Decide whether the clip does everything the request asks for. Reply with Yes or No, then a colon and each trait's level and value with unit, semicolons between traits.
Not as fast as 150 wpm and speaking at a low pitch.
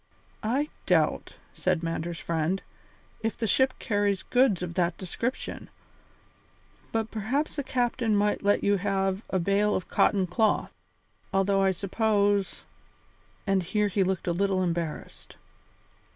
No: slow, 135 wpm; high, 200 Hz